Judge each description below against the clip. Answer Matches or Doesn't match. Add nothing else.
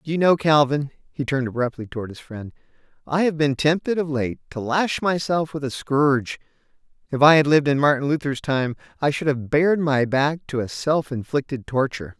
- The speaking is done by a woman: Doesn't match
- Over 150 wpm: Matches